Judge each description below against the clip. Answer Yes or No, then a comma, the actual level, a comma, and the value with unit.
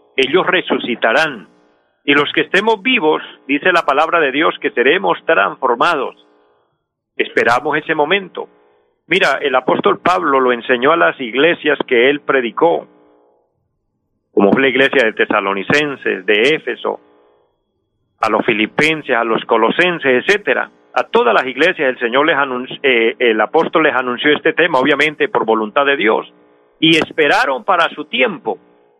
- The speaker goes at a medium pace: Yes, average, 145 wpm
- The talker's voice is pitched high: No, low, 125 Hz